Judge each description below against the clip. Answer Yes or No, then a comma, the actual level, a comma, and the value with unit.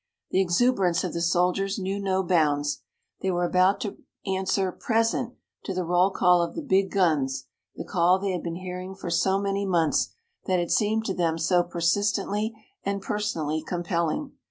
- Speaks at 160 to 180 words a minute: Yes, average, 175 wpm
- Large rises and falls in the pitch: No, narrow, 2.4 semitones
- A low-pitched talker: No, medium, 185 Hz